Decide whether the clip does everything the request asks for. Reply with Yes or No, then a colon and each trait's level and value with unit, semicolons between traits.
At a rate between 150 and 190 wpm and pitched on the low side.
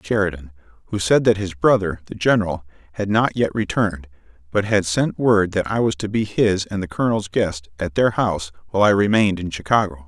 No: average, 200 wpm; very low, 95 Hz